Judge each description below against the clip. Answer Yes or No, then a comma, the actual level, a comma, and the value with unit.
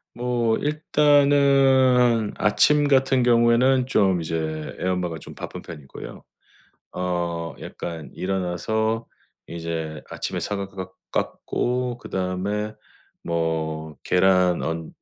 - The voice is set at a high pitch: No, very low, 95 Hz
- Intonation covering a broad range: Yes, wide, 6.7 semitones